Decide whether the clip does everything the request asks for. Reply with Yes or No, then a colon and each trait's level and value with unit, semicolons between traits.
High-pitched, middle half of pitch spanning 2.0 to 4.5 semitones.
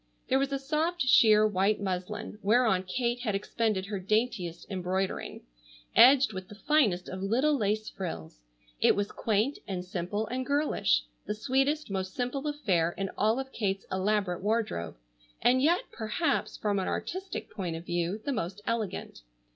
No: high, 210 Hz; average, 5.3 semitones